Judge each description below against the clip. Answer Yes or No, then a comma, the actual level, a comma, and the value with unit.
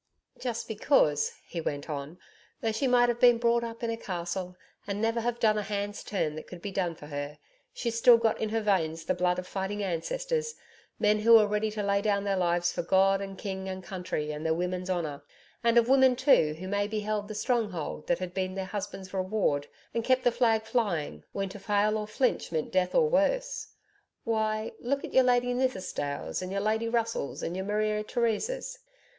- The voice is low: No, high, 205 Hz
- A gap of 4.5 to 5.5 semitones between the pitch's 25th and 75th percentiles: No, average, 4.1 semitones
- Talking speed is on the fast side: Yes, fast, 210 wpm